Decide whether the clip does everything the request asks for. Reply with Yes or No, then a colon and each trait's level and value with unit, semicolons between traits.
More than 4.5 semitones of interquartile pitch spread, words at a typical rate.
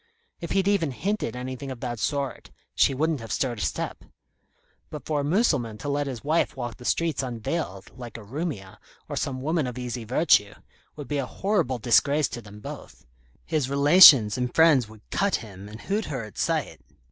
Yes: average, 4.9 semitones; average, 195 wpm